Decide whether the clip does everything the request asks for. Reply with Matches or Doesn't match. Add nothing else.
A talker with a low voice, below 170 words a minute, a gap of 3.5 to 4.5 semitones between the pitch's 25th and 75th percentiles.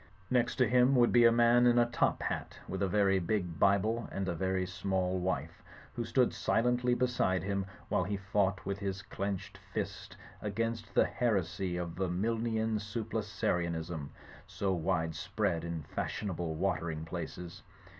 Matches